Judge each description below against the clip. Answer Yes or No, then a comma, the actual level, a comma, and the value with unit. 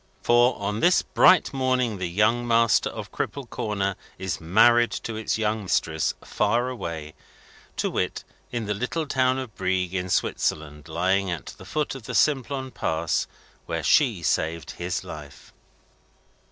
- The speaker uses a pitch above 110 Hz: No, low, 105 Hz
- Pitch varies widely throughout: Yes, wide, 5.9 semitones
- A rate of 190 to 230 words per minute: No, average, 155 wpm